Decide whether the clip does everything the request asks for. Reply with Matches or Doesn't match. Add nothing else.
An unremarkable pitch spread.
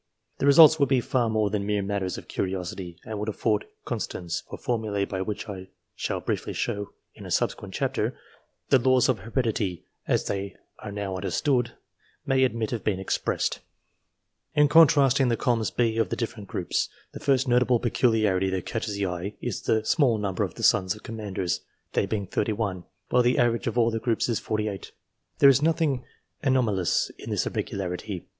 Matches